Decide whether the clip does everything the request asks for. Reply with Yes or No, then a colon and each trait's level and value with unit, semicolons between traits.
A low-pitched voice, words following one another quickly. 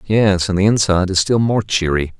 Yes: very low, 95 Hz; fast, 220 wpm